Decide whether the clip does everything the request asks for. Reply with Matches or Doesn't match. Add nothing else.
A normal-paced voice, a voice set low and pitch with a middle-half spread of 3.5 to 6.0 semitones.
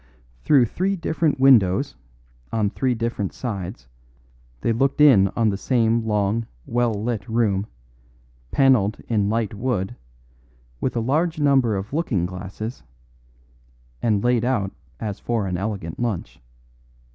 Doesn't match